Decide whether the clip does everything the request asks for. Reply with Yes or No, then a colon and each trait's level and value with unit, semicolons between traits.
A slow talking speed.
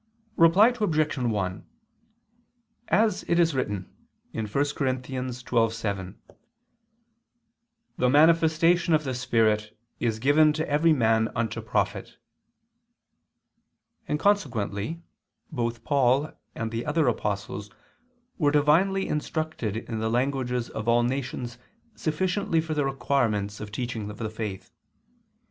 Yes: slow, 115 wpm